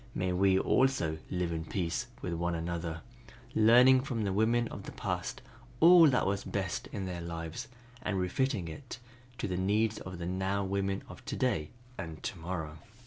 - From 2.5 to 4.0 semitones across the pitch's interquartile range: No, average, 4.5 semitones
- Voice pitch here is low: Yes, very low, 95 Hz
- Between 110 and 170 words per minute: No, average, 180 wpm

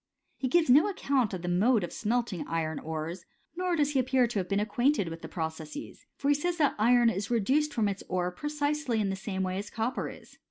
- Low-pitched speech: No, high, 225 Hz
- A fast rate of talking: Yes, fast, 235 wpm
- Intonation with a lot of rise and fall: Yes, wide, 7.3 semitones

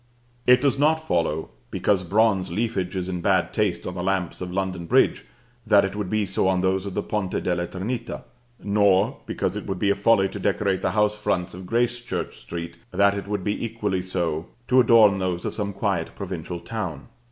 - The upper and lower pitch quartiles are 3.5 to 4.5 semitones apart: No, narrow, 2.6 semitones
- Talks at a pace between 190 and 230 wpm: Yes, average, 200 wpm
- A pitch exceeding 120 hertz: No, very low, 95 Hz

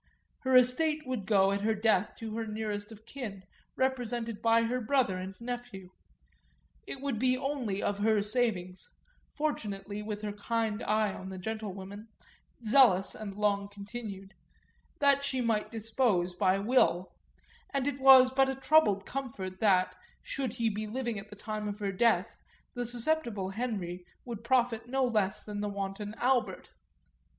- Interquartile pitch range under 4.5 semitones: Yes, average, 3.8 semitones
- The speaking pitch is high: Yes, high, 220 Hz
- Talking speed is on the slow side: No, average, 160 wpm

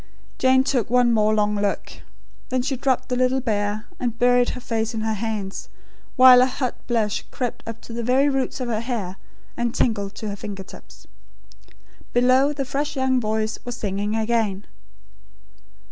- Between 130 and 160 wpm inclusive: No, average, 175 wpm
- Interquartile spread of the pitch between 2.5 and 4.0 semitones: Yes, average, 3.0 semitones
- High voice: Yes, high, 235 Hz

